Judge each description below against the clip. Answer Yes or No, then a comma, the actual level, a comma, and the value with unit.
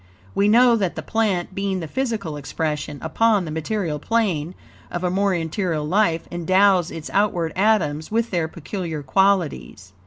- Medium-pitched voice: Yes, medium, 180 Hz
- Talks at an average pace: Yes, average, 155 wpm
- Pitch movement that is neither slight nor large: Yes, average, 4.2 semitones